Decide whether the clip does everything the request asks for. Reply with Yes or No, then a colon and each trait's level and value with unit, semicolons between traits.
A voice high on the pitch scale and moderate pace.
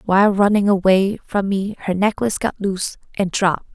Yes: high, 195 Hz; average, 175 wpm